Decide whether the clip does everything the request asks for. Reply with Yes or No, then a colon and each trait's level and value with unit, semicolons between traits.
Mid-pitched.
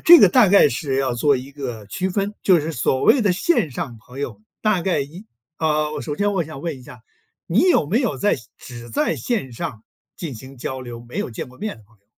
Yes: medium, 150 Hz